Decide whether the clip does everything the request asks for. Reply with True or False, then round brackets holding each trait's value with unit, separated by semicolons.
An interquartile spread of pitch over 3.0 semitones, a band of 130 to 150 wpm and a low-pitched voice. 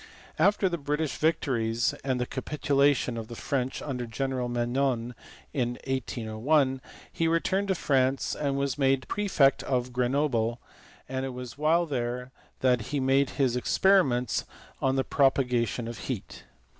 False (2.7 semitones; 145 wpm; 130 Hz)